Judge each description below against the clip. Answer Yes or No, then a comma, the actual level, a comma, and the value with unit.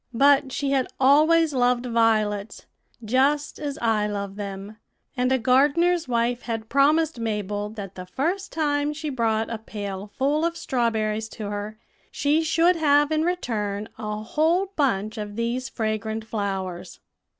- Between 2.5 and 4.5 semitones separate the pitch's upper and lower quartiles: No, wide, 5.5 semitones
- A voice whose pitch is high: Yes, high, 235 Hz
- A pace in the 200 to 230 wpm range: No, average, 150 wpm